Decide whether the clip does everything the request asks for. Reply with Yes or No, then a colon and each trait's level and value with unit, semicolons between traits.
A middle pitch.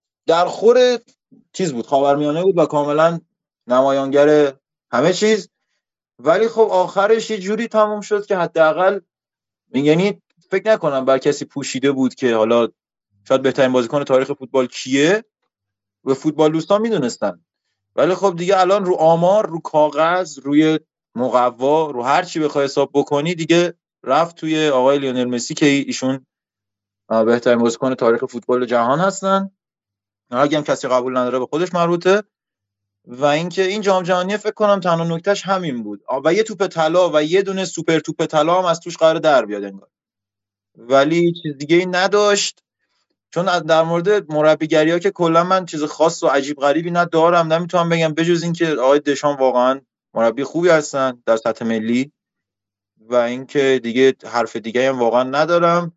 Yes: medium, 155 Hz